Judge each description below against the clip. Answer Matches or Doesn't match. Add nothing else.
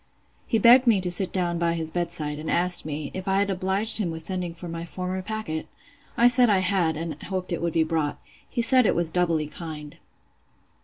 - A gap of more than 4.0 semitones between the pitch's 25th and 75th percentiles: Doesn't match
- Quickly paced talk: Matches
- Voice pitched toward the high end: Doesn't match